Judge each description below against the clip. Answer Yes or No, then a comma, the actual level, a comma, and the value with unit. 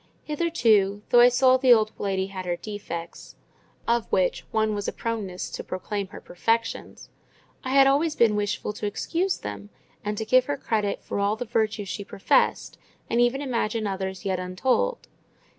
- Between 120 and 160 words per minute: No, average, 175 wpm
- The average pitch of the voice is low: No, high, 215 Hz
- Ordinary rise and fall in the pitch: Yes, average, 3.9 semitones